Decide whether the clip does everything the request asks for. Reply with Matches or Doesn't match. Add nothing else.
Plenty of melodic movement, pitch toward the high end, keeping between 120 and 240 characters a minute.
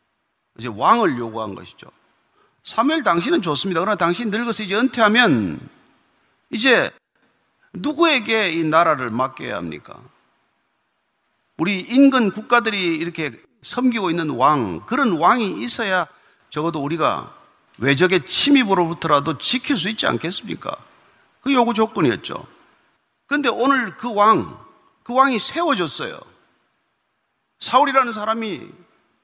Doesn't match